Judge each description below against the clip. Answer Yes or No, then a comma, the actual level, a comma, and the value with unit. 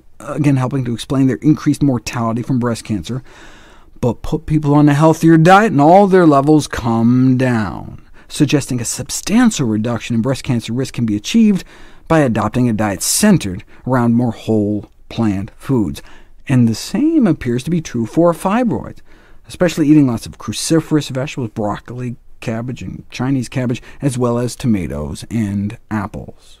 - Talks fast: No, average, 160 wpm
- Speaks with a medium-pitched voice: No, low, 125 Hz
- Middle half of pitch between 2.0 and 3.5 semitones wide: No, average, 5.1 semitones